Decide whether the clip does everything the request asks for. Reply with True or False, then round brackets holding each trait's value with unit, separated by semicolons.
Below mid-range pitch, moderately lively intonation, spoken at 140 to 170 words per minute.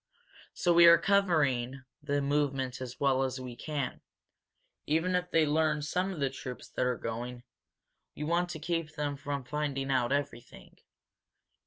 False (145 Hz; 3.5 semitones; 160 wpm)